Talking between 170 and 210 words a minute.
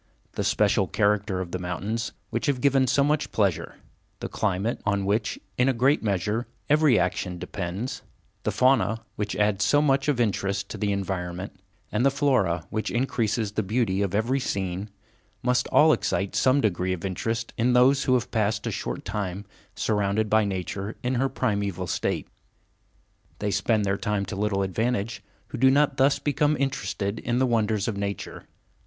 Yes: average, 175 wpm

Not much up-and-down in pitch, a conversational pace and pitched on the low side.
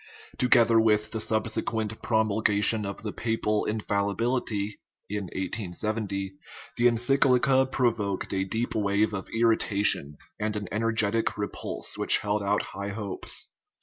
No: narrow, 2.1 semitones; slow, 125 wpm; low, 105 Hz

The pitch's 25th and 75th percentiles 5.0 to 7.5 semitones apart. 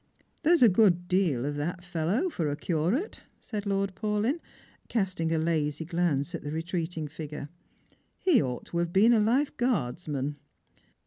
Yes: wide, 5.5 semitones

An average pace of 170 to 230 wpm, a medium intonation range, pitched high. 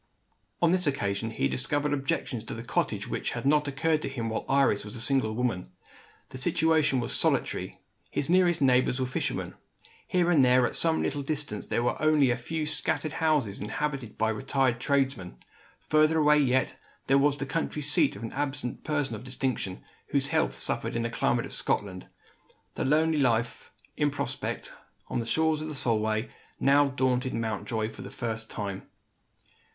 No: average, 180 wpm; average, 4.4 semitones; low, 135 Hz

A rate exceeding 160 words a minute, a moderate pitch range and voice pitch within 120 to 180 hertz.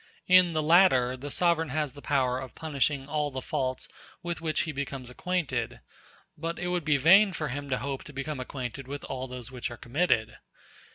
Yes: average, 195 wpm; average, 3.8 semitones; medium, 140 Hz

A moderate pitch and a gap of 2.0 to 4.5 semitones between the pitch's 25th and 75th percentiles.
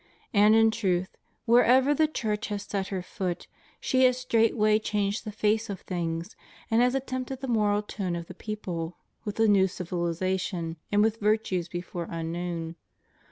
No: high, 205 Hz; average, 3.9 semitones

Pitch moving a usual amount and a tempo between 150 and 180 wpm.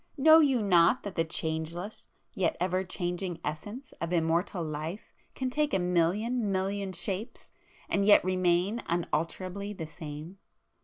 No: average, 3.4 semitones; average, 140 wpm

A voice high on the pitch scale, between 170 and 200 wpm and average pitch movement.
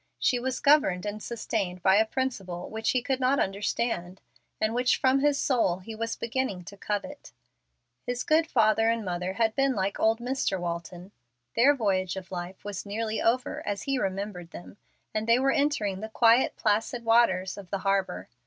Yes: high, 220 Hz; average, 180 wpm; average, 4.6 semitones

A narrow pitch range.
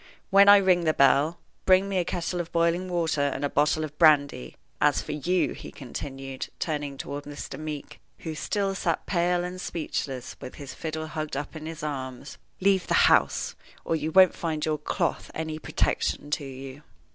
No: average, 3.4 semitones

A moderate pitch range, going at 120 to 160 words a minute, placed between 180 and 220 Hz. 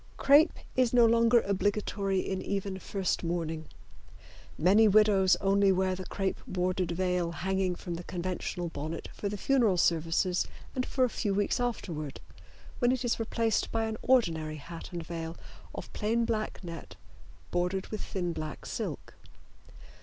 Yes: average, 4.0 semitones; average, 155 wpm; high, 190 Hz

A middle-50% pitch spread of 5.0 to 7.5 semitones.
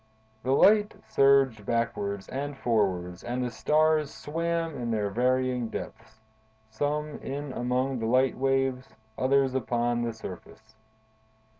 No: average, 3.2 semitones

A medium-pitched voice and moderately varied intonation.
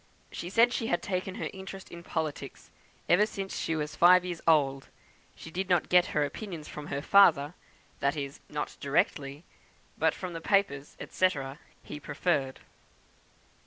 Yes: medium, 170 Hz; average, 4.1 semitones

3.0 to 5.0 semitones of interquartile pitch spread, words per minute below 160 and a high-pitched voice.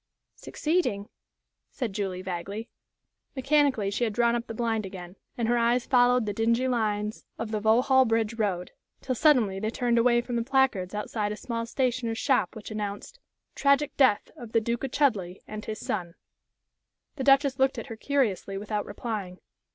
No: average, 3.4 semitones; average, 175 wpm; high, 230 Hz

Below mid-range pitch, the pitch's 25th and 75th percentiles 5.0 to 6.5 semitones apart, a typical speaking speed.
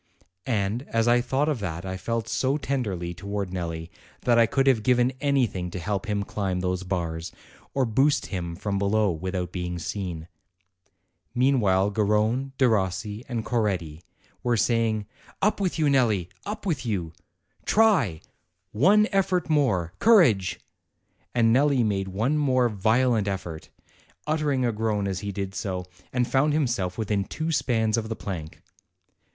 Yes: low, 110 Hz; wide, 5.5 semitones; average, 155 wpm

